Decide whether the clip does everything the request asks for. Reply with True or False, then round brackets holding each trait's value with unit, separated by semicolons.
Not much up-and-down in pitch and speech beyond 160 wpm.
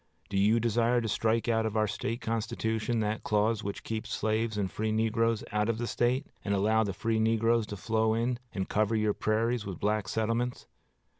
True (1.4 semitones; 200 wpm)